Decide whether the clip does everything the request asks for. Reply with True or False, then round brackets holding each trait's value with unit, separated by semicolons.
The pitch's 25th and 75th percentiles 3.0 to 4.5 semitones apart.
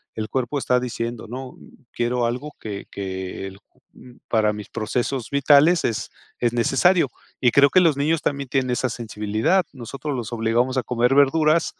True (3.8 semitones)